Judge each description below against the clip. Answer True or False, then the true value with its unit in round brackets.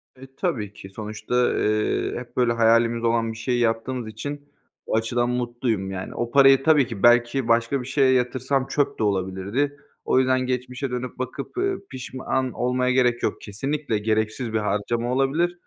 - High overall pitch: False (120 Hz)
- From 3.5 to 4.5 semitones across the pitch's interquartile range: False (2.7 semitones)